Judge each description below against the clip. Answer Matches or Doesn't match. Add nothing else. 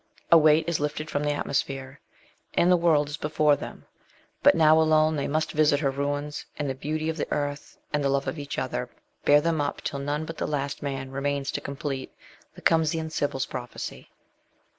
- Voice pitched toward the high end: Doesn't match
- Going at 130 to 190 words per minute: Doesn't match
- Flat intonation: Matches